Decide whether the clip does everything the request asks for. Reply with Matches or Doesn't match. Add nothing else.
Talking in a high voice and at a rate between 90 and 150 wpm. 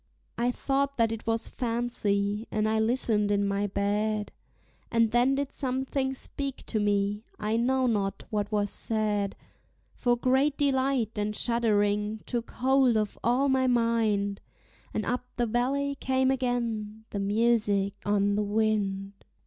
Matches